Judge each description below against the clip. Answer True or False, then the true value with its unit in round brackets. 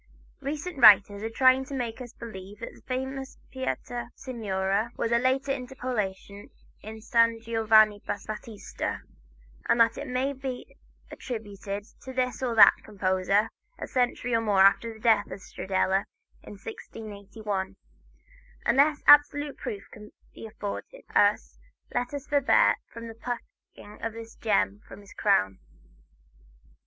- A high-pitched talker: True (225 Hz)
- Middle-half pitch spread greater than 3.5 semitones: True (3.9 semitones)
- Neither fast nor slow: False (130 wpm)